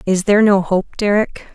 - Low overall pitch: No, high, 200 Hz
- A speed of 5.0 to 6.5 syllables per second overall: Yes, 5.2 syllables/s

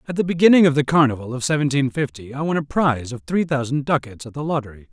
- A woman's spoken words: No, male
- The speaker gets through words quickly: Yes, fast, 245 wpm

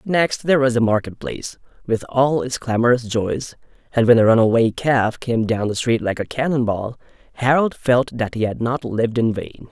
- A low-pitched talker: Yes, low, 120 Hz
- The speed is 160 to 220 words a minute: Yes, fast, 205 wpm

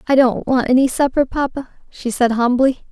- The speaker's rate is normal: Yes, average, 185 wpm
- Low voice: No, very high, 255 Hz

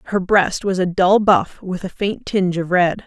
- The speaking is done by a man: No, female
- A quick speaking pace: Yes, fast, 235 wpm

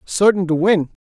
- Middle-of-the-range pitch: Yes, medium, 180 Hz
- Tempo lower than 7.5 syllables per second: Yes, 4.8 syllables/s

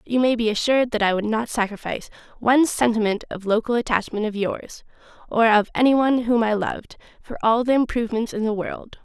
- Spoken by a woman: Yes, female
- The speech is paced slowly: No, fast, 205 wpm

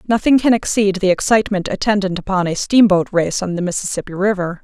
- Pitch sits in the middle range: No, high, 195 Hz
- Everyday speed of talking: Yes, average, 180 wpm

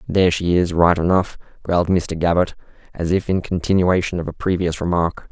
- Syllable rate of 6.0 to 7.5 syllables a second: No, 5.5 syllables/s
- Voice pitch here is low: Yes, very low, 90 Hz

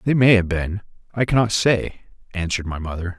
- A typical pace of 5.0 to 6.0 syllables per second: Yes, 5.9 syllables/s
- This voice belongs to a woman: No, male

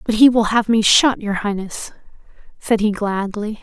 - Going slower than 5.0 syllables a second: Yes, 4.6 syllables/s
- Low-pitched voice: No, high, 215 Hz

